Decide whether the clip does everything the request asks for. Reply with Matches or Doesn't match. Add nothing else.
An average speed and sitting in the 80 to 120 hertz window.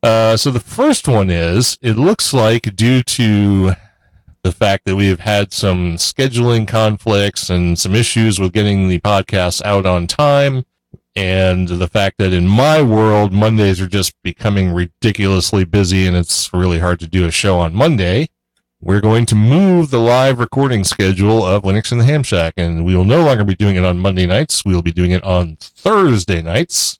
Matches